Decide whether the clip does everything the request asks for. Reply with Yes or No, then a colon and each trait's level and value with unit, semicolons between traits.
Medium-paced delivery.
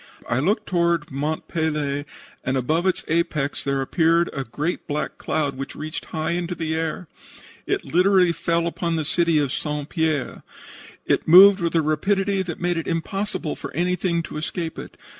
Yes: average, 175 wpm